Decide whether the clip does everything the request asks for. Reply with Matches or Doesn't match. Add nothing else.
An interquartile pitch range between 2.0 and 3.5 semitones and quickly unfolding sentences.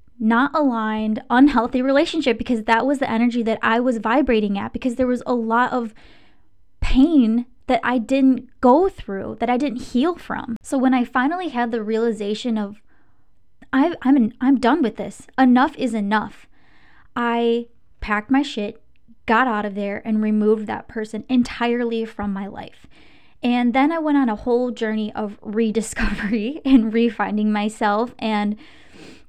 Doesn't match